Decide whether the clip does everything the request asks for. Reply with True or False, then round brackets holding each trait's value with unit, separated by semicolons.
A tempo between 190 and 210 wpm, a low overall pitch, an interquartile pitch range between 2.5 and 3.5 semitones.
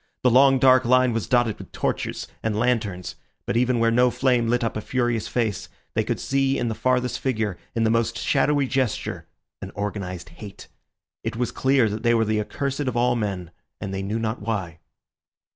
True (195 wpm; 115 Hz; 3.1 semitones)